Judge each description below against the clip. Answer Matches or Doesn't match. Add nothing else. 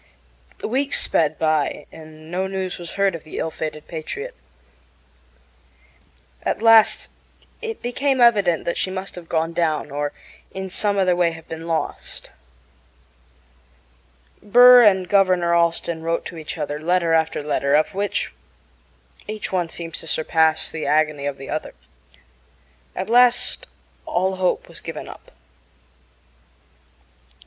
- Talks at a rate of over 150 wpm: Doesn't match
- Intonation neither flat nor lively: Matches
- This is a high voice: Doesn't match